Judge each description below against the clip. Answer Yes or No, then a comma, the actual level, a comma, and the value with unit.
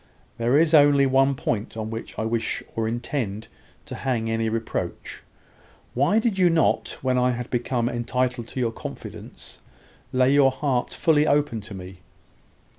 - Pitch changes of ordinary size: Yes, average, 3.7 semitones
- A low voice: Yes, low, 125 Hz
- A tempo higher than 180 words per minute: No, average, 160 wpm